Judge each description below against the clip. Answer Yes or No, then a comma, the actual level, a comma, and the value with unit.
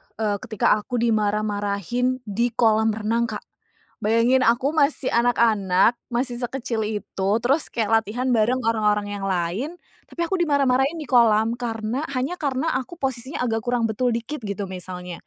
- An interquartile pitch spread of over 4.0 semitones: No, average, 3.1 semitones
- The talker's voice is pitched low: No, high, 230 Hz